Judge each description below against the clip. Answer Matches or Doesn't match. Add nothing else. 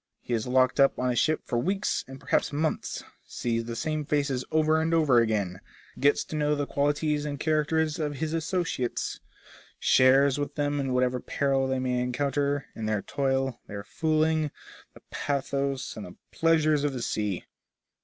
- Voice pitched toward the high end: Doesn't match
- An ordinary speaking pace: Matches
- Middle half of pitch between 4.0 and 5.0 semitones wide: Doesn't match